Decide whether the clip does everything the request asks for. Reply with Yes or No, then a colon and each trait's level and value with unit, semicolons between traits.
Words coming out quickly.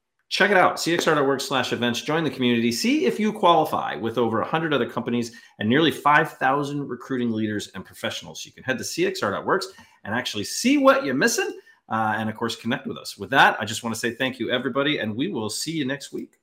Yes: fast, 220 wpm